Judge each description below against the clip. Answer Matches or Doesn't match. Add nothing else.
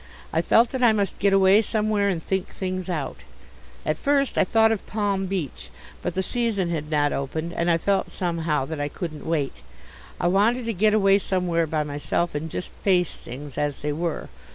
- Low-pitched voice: Doesn't match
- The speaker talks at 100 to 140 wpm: Doesn't match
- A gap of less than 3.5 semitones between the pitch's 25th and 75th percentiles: Doesn't match